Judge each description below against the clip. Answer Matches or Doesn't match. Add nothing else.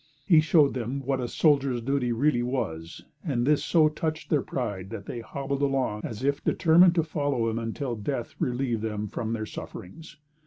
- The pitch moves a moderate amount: Matches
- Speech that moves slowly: Doesn't match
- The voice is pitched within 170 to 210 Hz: Doesn't match